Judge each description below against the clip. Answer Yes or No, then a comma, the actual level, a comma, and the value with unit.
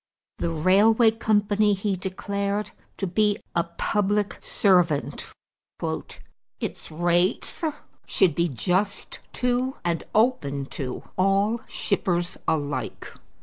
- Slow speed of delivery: Yes, slow, 100 wpm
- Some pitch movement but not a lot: Yes, average, 3.4 semitones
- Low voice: No, high, 195 Hz